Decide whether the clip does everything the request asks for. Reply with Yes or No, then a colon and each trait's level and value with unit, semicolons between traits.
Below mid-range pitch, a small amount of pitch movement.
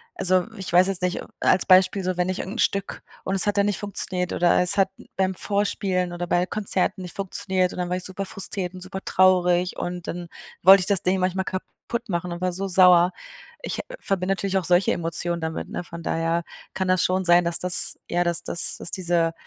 No: medium, 185 Hz; narrow, 1.4 semitones